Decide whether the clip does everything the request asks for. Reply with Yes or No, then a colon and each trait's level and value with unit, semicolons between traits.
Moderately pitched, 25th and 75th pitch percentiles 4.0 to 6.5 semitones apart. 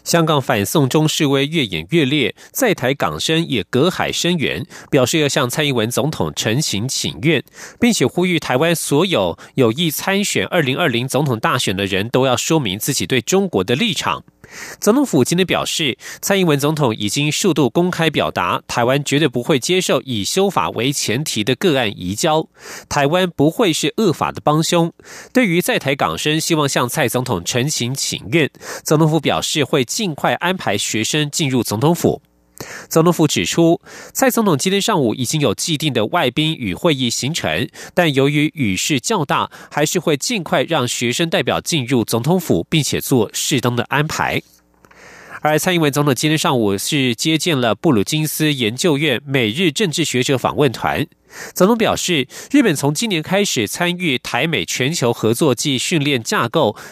Yes: medium, 150 Hz; average, 5.1 semitones